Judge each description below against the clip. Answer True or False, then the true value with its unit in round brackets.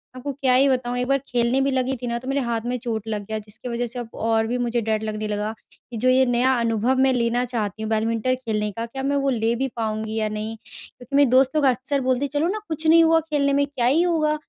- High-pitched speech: True (245 Hz)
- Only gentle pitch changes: False (3.2 semitones)